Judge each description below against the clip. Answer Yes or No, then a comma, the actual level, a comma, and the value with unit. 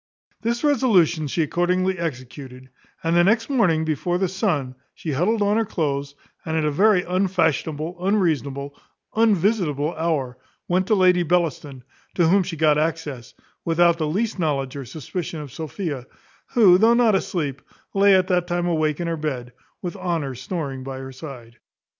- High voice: No, medium, 165 Hz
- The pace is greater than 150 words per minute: Yes, average, 165 wpm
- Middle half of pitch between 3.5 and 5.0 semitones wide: Yes, average, 4.6 semitones